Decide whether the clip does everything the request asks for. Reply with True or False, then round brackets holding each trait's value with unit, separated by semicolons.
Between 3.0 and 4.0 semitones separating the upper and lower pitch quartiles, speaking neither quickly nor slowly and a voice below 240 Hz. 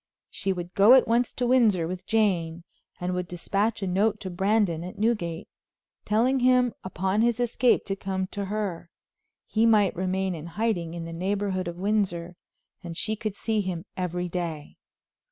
True (3.7 semitones; 170 wpm; 190 Hz)